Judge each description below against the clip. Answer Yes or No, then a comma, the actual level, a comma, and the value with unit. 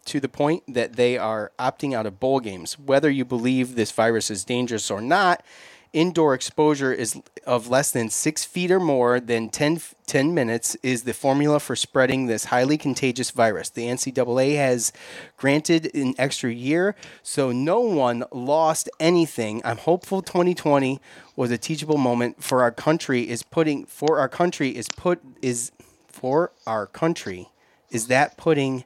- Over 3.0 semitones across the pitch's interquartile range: Yes, average, 3.9 semitones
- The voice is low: Yes, low, 130 Hz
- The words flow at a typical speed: Yes, average, 165 wpm